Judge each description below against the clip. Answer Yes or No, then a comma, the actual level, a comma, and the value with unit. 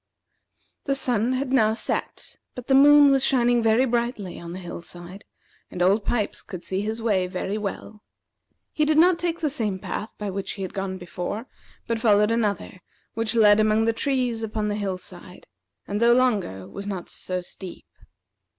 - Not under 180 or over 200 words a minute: Yes, average, 185 wpm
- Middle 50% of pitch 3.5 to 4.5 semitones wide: Yes, average, 4.1 semitones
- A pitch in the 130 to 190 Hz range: No, high, 215 Hz